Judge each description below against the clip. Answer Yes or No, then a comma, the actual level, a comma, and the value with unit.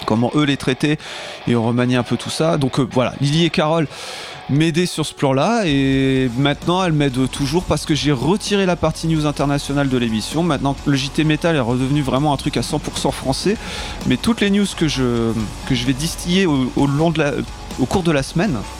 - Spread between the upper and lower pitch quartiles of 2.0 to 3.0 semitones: No, average, 3.8 semitones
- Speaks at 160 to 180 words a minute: No, average, 215 wpm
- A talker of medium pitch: Yes, medium, 145 Hz